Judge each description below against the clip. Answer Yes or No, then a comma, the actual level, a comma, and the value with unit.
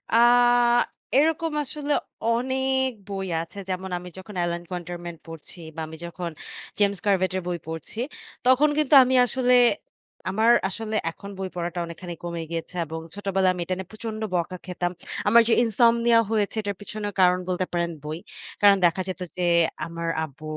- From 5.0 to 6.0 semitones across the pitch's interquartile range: No, average, 4.6 semitones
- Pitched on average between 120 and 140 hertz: No, high, 190 Hz